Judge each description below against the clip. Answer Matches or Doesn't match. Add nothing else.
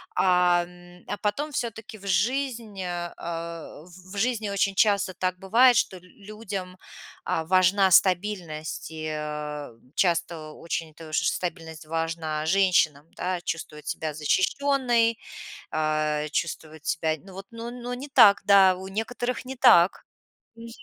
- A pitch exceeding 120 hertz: Matches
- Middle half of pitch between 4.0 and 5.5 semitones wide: Matches